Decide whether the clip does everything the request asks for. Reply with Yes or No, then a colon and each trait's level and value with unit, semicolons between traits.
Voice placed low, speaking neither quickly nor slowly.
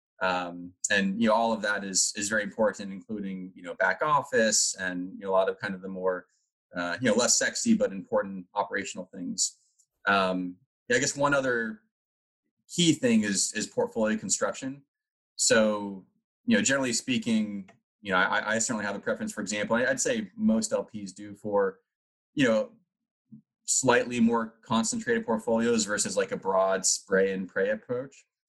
Yes: low, 115 Hz; average, 175 wpm